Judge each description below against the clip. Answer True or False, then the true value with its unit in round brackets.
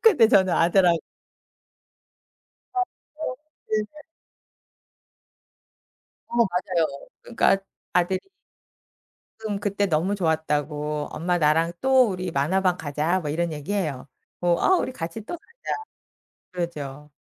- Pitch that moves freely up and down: False (4.9 semitones)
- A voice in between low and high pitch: True (175 Hz)